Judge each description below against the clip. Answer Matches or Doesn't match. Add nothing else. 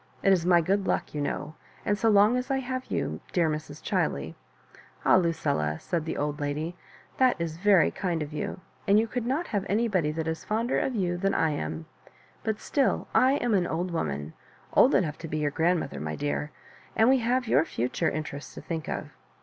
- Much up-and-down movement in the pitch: Matches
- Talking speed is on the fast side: Matches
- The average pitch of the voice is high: Doesn't match